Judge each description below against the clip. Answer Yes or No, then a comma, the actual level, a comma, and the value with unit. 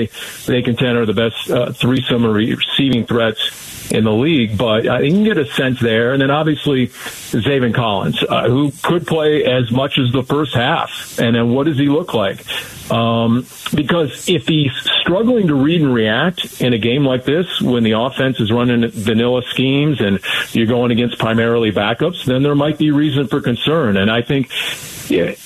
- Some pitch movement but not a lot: Yes, average, 3.8 semitones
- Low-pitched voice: Yes, low, 125 Hz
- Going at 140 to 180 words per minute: No, average, 190 wpm